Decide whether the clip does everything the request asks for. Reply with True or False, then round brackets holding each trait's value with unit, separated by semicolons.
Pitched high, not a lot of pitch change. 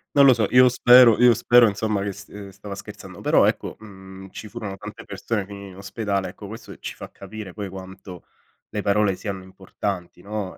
False (100 Hz; 2.1 semitones)